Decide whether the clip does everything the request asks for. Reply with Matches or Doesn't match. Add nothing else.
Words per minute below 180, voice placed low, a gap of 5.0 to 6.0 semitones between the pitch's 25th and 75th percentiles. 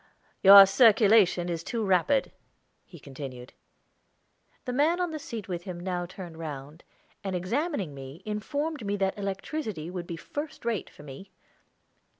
Doesn't match